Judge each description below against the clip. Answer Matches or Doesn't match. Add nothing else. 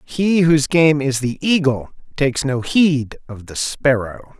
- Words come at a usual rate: Matches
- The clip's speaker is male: Matches